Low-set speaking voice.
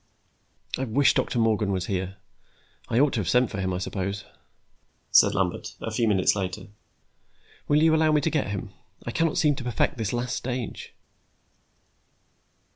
Yes: low, 115 Hz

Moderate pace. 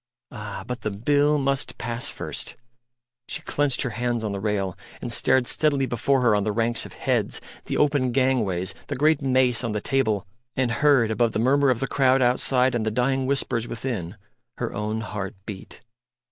Yes: average, 190 wpm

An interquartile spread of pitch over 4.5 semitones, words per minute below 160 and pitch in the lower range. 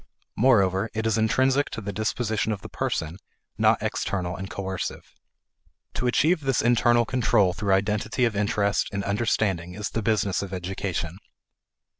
No: average, 3.2 semitones; average, 150 wpm; low, 105 Hz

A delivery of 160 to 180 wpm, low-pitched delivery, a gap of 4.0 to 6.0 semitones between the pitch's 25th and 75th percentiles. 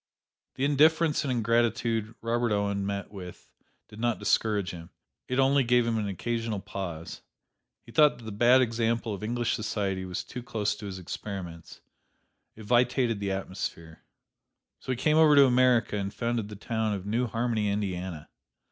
No: average, 165 wpm; low, 110 Hz; average, 3.4 semitones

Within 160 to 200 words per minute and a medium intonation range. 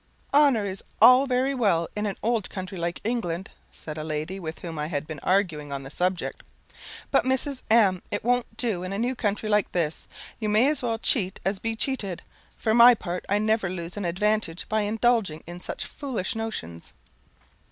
Yes: average, 195 wpm; average, 4.9 semitones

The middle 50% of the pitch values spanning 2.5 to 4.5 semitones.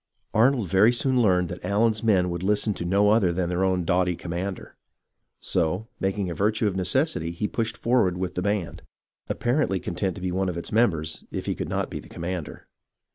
Yes: average, 3.4 semitones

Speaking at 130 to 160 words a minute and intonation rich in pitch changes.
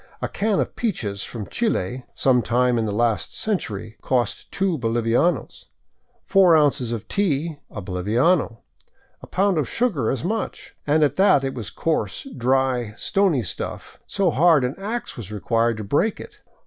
No: average, 175 wpm; wide, 7.5 semitones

